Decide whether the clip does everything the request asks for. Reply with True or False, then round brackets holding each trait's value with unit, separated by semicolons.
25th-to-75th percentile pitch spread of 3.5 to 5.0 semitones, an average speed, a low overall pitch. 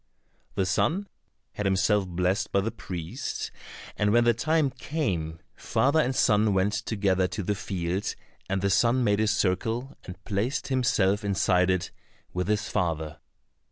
True (4.1 semitones; 155 wpm; 100 Hz)